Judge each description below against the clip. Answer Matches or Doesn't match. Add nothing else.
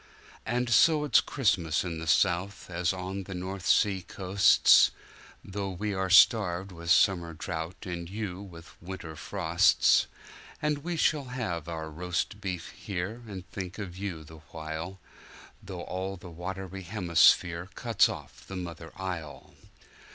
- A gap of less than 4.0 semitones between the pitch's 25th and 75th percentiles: Matches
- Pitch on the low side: Matches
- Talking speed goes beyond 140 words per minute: Doesn't match